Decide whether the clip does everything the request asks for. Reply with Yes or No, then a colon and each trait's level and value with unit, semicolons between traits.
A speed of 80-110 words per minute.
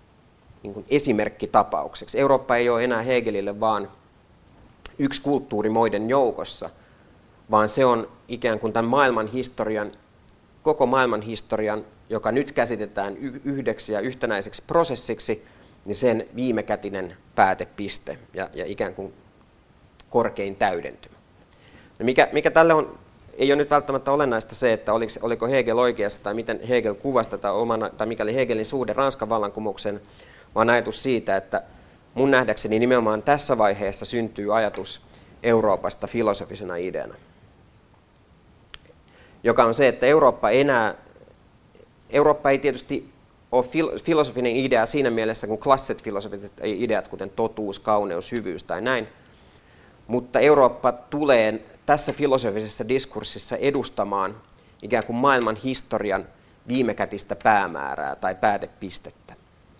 No: average, 120 wpm